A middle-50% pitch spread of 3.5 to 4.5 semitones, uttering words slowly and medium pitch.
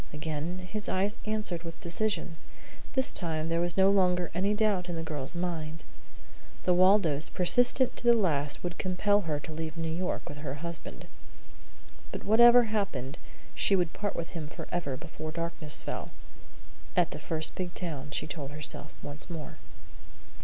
No: average, 3.8 semitones; average, 165 wpm; medium, 170 Hz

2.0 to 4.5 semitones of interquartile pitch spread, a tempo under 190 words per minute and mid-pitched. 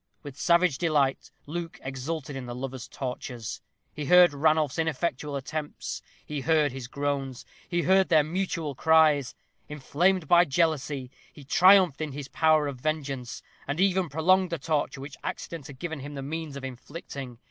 Yes: average, 3.4 semitones; average, 160 wpm; medium, 150 Hz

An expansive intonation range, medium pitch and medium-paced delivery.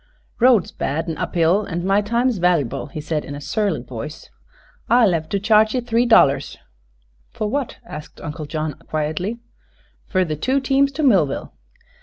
Yes: wide, 7.0 semitones; medium, 180 Hz; average, 170 wpm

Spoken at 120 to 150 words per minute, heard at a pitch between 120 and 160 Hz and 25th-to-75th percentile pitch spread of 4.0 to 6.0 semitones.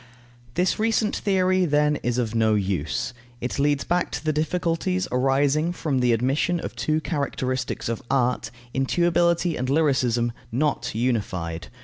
Yes: average, 140 wpm; medium, 140 Hz; wide, 5.6 semitones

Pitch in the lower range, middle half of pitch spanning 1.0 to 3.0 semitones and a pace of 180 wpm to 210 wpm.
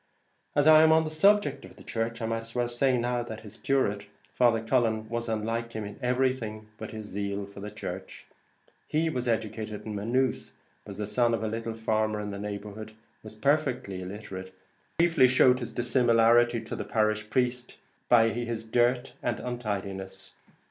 Yes: low, 115 Hz; narrow, 2.5 semitones; average, 185 wpm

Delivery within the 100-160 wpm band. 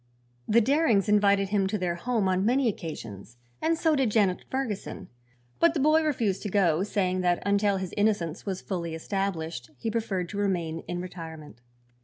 No: average, 175 wpm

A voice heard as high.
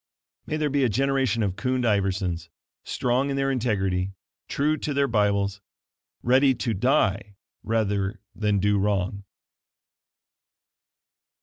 No: low, 105 Hz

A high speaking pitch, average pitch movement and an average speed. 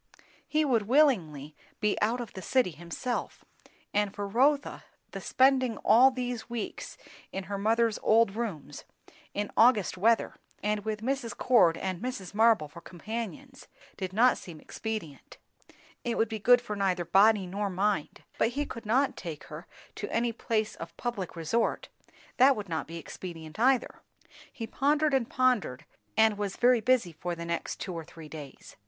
Yes: high, 215 Hz; average, 5.0 semitones; average, 165 wpm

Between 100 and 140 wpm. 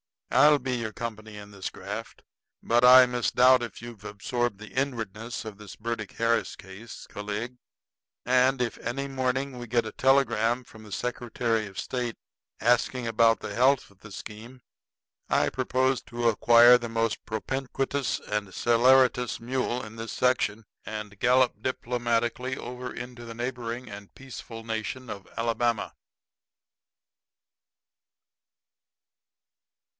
Yes: slow, 135 wpm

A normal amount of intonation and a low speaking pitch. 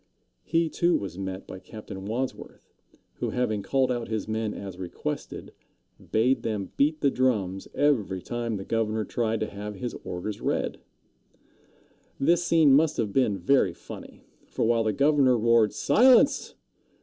Yes: average, 4.9 semitones; low, 115 Hz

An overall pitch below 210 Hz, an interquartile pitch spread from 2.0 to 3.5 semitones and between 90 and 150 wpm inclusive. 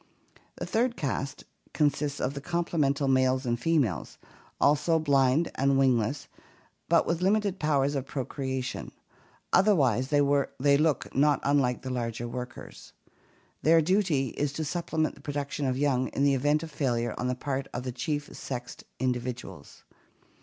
Yes: medium, 140 Hz; average, 2.9 semitones; average, 145 wpm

